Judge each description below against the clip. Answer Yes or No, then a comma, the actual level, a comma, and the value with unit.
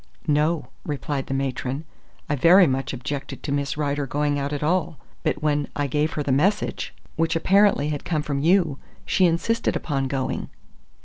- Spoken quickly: No, average, 170 wpm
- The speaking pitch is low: No, medium, 145 Hz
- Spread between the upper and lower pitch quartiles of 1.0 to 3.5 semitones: Yes, average, 2.8 semitones